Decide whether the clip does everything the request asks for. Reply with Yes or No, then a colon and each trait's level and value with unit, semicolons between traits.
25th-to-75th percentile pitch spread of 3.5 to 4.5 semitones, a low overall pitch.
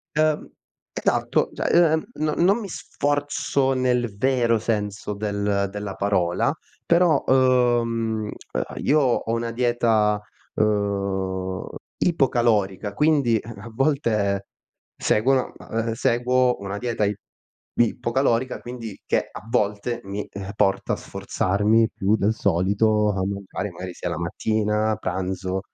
Yes: average, 3.9 semitones; low, 110 Hz